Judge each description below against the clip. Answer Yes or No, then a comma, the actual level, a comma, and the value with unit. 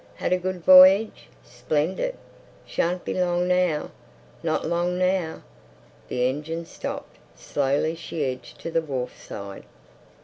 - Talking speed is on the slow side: Yes, slow, 130 wpm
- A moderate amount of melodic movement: Yes, average, 3.7 semitones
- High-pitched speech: No, medium, 170 Hz